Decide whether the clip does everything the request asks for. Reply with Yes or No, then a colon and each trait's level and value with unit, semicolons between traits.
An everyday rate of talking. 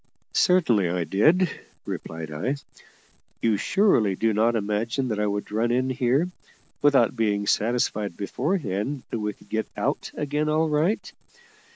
Yes: average, 145 wpm